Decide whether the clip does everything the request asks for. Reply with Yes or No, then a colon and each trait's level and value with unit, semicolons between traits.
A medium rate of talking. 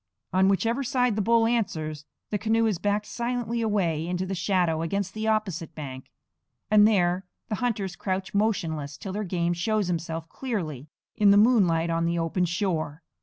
Yes: average, 170 wpm